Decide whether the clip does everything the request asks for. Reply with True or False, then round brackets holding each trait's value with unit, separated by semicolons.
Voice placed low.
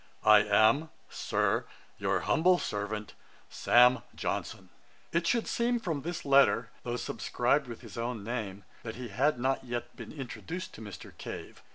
True (125 Hz)